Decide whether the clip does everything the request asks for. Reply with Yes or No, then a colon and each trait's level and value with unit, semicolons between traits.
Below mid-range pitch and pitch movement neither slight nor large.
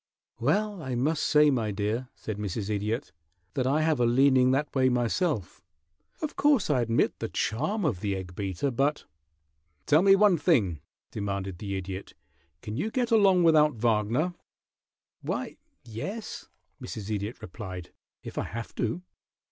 No: low, 120 Hz; wide, 7.1 semitones